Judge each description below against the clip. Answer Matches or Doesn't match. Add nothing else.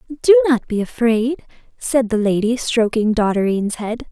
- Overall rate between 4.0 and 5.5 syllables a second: Matches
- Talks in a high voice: Matches